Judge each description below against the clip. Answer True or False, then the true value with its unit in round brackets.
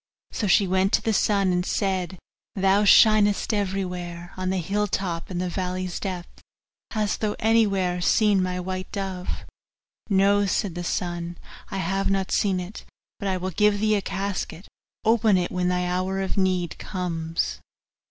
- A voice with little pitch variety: True (1.9 semitones)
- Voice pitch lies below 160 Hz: False (190 Hz)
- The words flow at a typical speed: True (165 wpm)